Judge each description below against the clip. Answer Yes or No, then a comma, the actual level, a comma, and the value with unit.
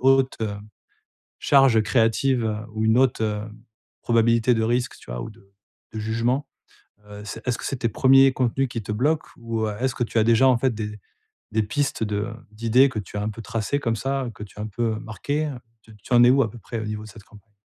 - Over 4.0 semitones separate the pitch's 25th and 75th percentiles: No, average, 3.1 semitones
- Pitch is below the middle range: Yes, low, 115 Hz